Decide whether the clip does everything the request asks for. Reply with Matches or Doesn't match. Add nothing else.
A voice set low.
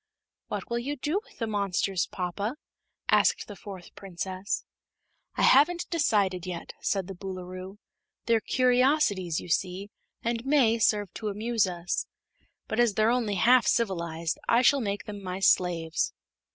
Doesn't match